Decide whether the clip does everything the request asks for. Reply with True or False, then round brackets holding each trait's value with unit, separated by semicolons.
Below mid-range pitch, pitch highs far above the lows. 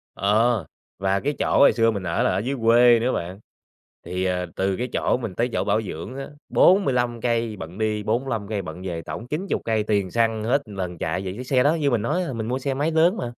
False (115 Hz; 4.5 semitones)